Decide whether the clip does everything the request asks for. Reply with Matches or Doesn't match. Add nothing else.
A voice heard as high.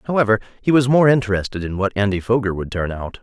Doesn't match